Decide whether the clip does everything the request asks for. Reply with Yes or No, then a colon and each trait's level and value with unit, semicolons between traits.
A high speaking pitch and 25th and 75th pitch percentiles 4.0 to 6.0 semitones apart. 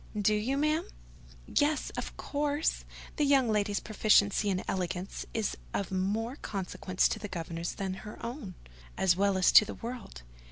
Yes: high, 210 Hz; average, 4.9 semitones